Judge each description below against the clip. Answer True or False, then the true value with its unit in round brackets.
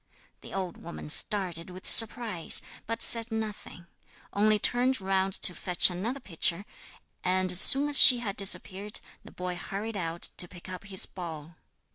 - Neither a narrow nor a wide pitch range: True (3.5 semitones)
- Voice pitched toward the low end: False (190 Hz)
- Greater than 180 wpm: False (160 wpm)